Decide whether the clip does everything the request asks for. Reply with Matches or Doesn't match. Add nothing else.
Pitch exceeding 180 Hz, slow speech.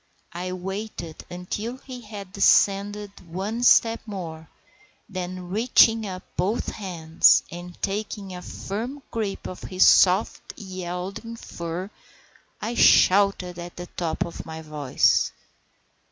Matches